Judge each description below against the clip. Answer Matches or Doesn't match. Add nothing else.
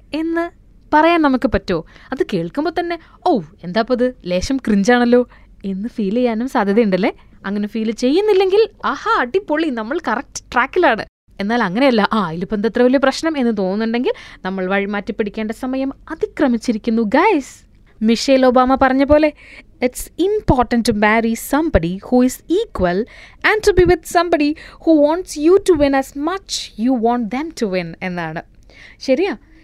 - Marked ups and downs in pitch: Matches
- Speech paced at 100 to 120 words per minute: Matches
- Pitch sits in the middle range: Doesn't match